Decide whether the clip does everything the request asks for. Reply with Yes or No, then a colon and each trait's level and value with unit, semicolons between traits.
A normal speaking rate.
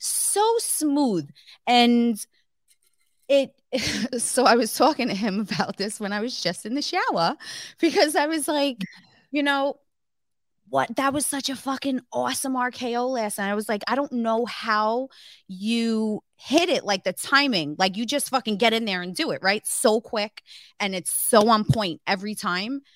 Yes: average, 180 wpm